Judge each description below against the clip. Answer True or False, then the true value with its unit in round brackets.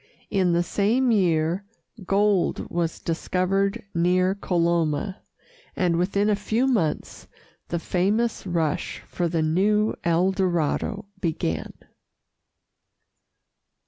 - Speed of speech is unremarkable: False (100 wpm)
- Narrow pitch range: False (3.1 semitones)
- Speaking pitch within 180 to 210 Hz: True (185 Hz)